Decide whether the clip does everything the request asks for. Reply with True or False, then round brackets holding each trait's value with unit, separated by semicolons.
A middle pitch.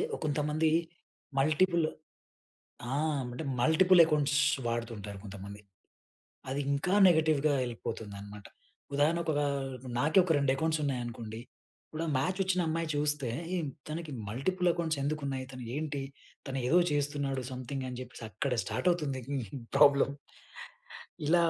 True (145 Hz)